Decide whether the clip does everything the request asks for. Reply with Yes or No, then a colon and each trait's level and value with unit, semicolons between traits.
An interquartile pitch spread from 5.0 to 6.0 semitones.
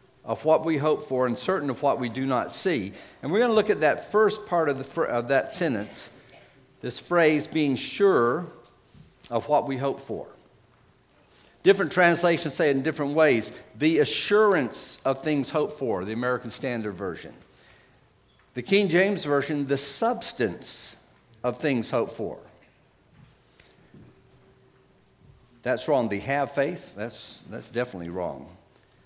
Yes: average, 5.3 semitones